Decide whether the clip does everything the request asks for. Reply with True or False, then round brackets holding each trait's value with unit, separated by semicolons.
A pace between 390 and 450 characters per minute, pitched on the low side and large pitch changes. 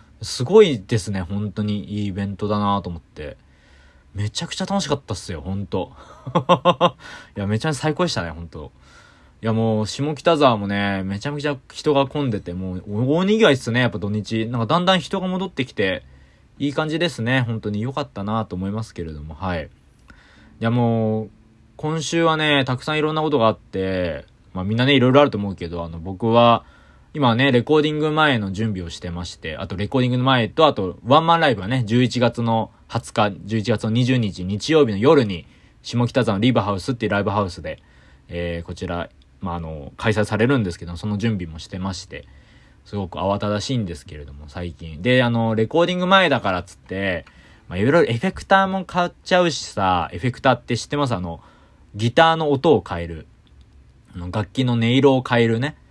True (395 characters per minute; 110 Hz; 6.7 semitones)